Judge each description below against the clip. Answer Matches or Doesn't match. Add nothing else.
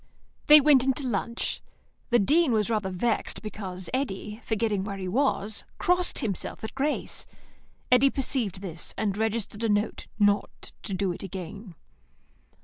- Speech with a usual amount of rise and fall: Matches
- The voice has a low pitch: Doesn't match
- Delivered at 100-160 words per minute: Matches